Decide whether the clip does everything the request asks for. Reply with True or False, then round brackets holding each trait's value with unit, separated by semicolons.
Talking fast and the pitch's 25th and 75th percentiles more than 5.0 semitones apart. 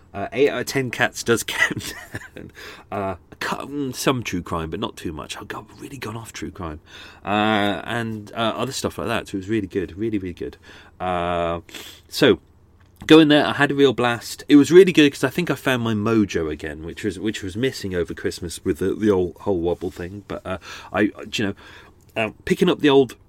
True (215 wpm; 5.4 semitones)